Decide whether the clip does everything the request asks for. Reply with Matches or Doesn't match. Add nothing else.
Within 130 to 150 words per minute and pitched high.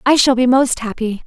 Doesn't match